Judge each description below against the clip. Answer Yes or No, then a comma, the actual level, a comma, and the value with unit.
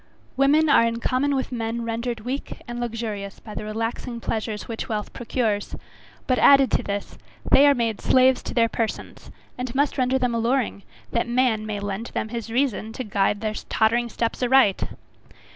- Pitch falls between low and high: No, high, 235 Hz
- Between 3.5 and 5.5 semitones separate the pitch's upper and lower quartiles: No, average, 2.7 semitones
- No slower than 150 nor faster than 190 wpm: Yes, average, 175 wpm